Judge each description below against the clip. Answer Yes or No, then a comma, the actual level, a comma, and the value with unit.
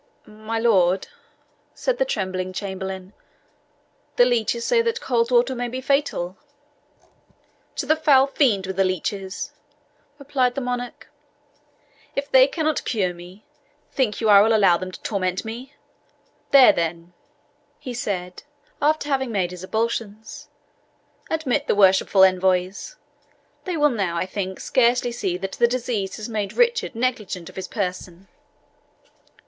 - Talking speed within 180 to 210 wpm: No, average, 140 wpm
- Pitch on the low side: No, high, 220 Hz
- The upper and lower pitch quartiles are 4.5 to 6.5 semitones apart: Yes, wide, 5.5 semitones